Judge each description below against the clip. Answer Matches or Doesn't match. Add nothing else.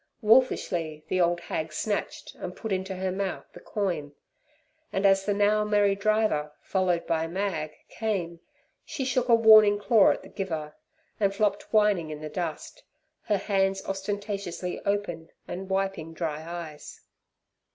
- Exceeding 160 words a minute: Doesn't match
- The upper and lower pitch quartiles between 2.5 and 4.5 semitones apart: Matches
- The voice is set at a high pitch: Matches